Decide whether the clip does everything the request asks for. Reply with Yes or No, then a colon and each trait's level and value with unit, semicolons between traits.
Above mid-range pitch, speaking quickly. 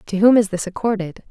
Yes: high, 200 Hz; fast, 230 wpm